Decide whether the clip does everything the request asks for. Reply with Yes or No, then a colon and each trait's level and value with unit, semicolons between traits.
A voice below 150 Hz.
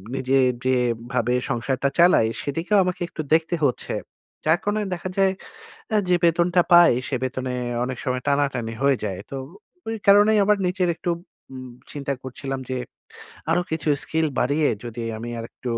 Yes: medium, 140 Hz